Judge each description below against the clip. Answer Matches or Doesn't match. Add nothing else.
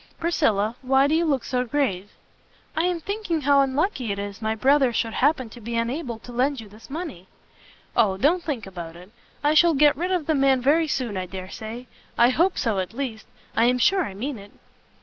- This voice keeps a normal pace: Doesn't match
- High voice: Matches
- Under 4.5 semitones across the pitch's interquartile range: Doesn't match